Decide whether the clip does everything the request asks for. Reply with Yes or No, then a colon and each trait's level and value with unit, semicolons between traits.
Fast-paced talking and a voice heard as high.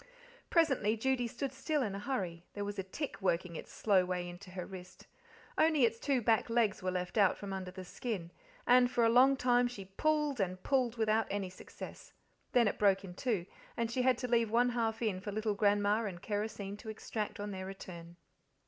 Yes: fast, 210 wpm; high, 215 Hz